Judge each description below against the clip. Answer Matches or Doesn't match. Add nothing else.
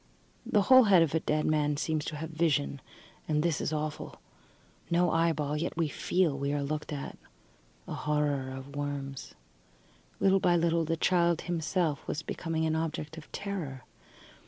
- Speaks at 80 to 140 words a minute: Doesn't match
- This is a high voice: Doesn't match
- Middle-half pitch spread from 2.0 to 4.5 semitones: Matches